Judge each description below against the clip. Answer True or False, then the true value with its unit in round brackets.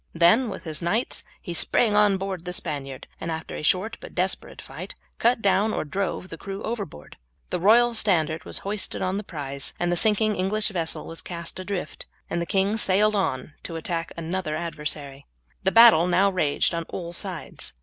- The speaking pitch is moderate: True (180 Hz)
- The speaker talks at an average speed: True (185 wpm)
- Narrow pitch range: False (3.8 semitones)